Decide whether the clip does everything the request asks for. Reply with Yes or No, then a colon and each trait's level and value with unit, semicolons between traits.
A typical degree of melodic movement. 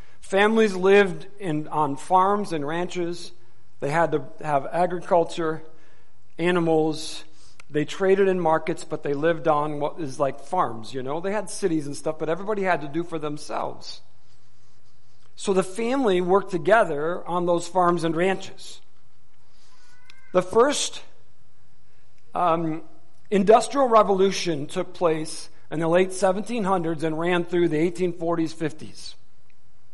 Yes: average, 4.3 semitones